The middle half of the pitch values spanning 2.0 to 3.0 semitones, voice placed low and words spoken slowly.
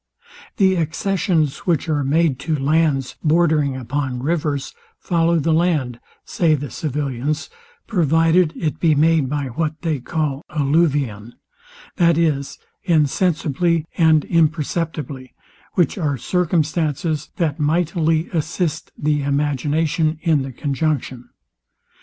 No: average, 2.7 semitones; medium, 155 Hz; slow, 110 wpm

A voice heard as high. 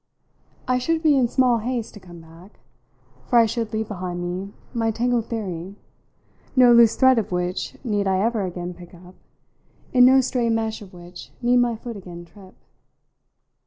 Yes: high, 220 Hz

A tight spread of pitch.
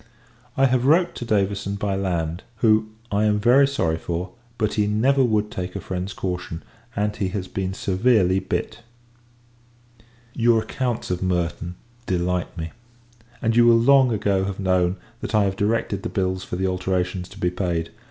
No: average, 3.4 semitones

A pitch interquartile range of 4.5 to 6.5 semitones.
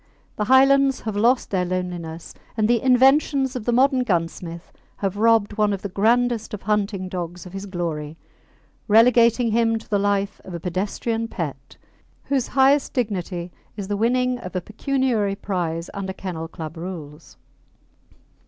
Yes: average, 5.0 semitones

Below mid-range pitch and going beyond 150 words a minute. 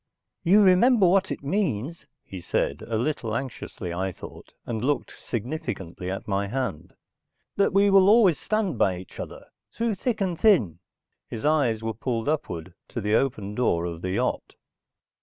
Yes: low, 125 Hz; average, 165 wpm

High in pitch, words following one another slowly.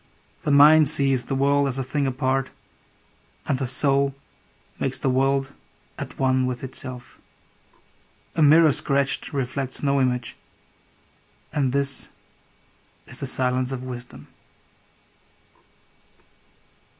No: low, 135 Hz; slow, 115 wpm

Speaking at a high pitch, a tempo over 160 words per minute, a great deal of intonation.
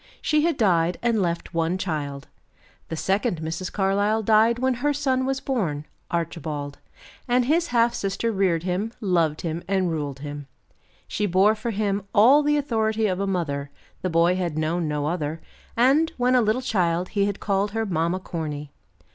Yes: high, 195 Hz; average, 175 wpm; wide, 5.7 semitones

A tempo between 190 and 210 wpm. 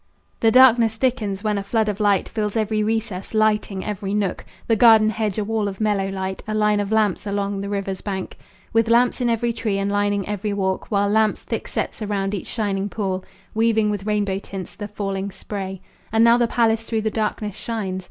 Yes: fast, 205 wpm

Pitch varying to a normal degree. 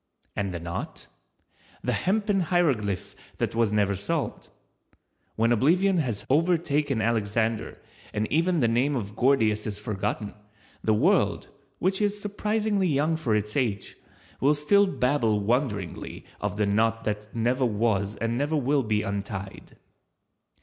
No: wide, 6.8 semitones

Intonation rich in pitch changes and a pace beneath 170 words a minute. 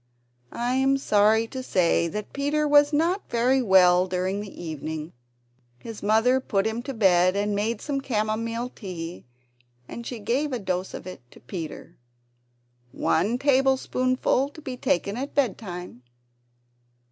Yes: wide, 5.9 semitones; average, 150 wpm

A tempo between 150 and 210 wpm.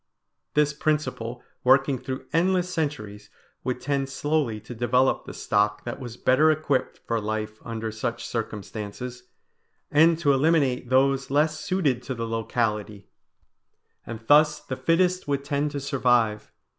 No: average, 140 wpm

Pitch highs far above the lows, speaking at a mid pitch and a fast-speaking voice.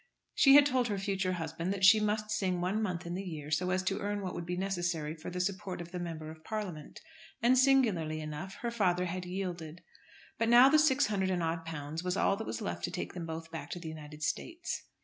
No: average, 4.1 semitones; medium, 180 Hz; fast, 240 wpm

